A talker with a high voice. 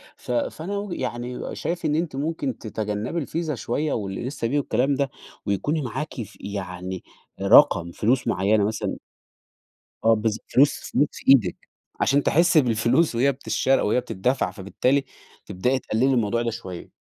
No: low, 125 Hz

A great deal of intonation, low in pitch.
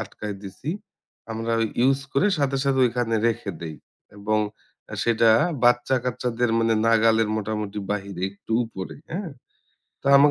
No: average, 2.9 semitones; low, 115 Hz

